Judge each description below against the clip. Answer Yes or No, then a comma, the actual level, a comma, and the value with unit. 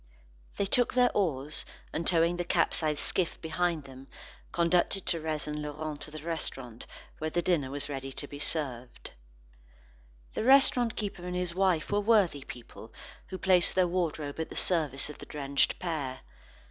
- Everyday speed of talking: Yes, average, 165 wpm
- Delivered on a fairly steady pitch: No, average, 3.8 semitones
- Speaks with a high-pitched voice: No, medium, 160 Hz